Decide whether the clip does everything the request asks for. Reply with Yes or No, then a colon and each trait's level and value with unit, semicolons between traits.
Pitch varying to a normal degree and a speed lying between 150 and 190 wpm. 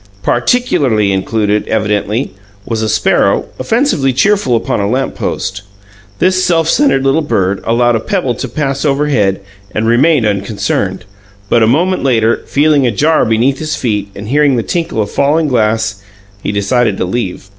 No: wide, 5.8 semitones; average, 160 wpm